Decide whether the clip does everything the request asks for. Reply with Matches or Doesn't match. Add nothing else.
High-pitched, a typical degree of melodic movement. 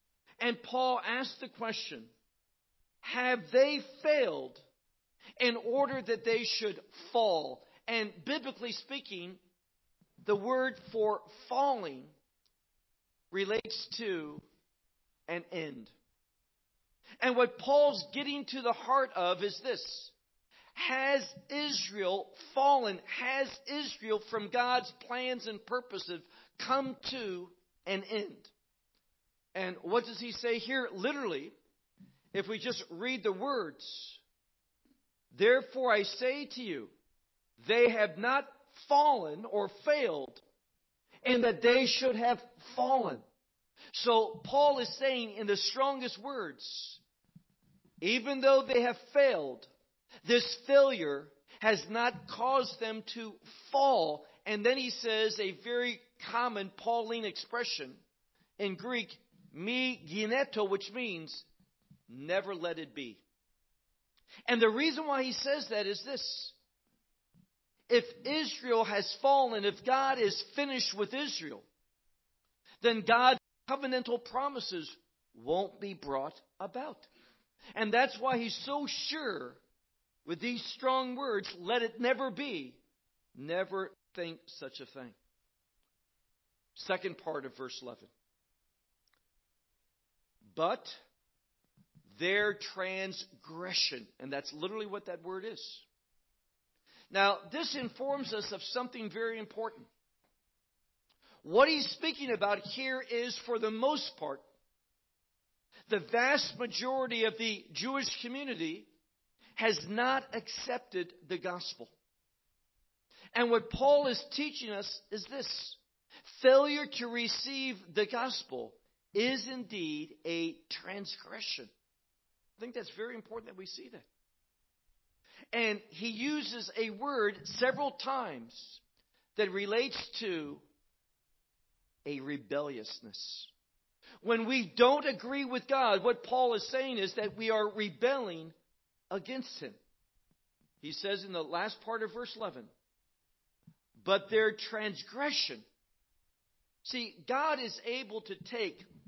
Matches